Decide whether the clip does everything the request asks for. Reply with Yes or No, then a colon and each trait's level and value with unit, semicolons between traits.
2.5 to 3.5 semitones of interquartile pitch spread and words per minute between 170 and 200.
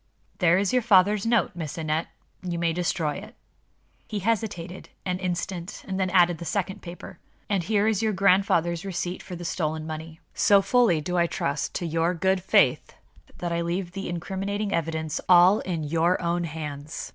Yes: average, 2.8 semitones; average, 180 wpm